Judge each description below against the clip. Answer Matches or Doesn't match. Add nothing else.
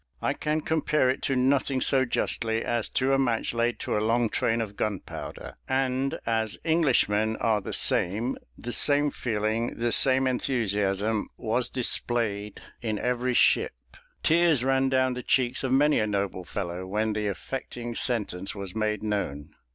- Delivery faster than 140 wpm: Matches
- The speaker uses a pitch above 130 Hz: Doesn't match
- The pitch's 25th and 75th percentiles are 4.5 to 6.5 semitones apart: Doesn't match